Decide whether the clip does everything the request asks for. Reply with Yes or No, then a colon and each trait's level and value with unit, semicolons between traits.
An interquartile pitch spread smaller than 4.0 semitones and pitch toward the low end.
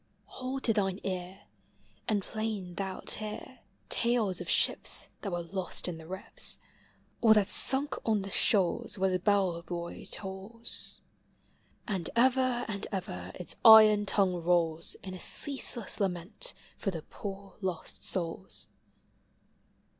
No: average, 3.5 semitones; high, 195 Hz